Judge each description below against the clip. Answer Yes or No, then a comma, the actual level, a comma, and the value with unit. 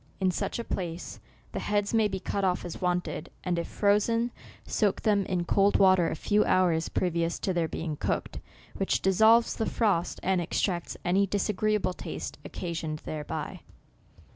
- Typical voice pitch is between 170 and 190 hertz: Yes, medium, 185 Hz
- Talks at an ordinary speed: Yes, average, 165 wpm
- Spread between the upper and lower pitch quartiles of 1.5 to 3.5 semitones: Yes, average, 3.0 semitones